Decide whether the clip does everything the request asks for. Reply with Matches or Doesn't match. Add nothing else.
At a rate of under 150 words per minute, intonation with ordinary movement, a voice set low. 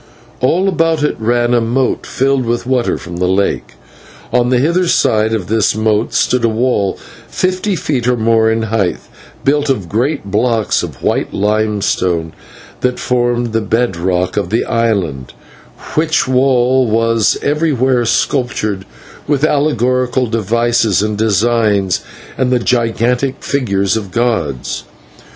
Matches